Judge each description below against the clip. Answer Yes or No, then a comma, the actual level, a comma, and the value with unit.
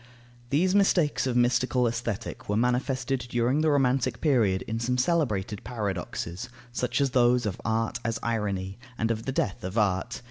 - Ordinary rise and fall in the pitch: Yes, average, 3.2 semitones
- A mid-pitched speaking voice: No, low, 120 Hz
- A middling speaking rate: Yes, average, 165 wpm